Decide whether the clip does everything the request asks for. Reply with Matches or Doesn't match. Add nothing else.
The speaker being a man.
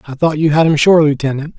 Matches